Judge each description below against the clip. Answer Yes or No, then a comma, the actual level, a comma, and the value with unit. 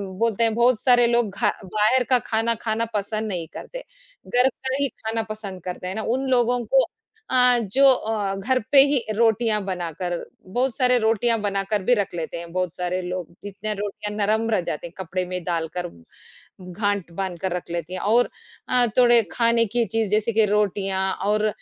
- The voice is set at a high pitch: Yes, high, 215 Hz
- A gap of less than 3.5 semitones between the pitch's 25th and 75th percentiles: No, average, 3.9 semitones